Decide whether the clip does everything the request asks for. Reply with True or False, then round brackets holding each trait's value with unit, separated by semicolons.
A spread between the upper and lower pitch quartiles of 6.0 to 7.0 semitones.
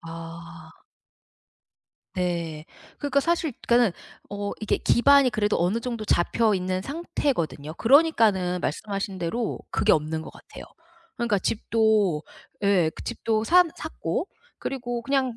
False (5.6 semitones)